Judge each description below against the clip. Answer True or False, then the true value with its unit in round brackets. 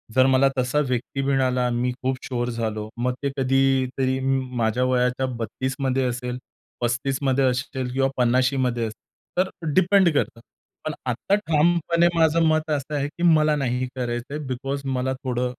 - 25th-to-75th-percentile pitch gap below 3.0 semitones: True (2.4 semitones)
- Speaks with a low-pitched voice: True (130 Hz)